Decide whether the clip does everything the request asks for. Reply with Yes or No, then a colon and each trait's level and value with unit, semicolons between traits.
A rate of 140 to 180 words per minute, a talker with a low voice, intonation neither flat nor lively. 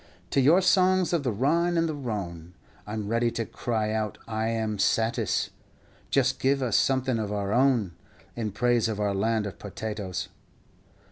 Yes: average, 175 wpm; low, 115 Hz; average, 4.2 semitones